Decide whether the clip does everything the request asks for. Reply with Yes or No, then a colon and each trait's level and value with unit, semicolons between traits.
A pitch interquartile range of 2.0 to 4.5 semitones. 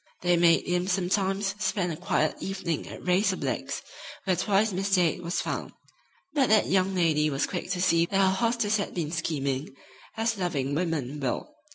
Yes: average, 3.0 semitones